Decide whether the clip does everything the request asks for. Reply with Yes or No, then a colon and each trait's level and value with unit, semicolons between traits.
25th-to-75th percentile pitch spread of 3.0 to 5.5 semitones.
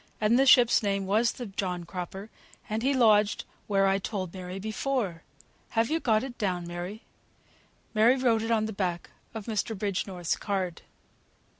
Yes: average, 3.3 semitones